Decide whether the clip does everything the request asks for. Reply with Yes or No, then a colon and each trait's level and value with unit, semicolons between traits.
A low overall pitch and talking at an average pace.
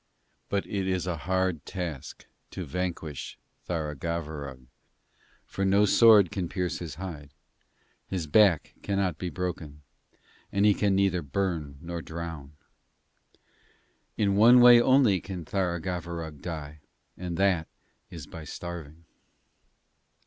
No: very low, 90 Hz; slow, 120 wpm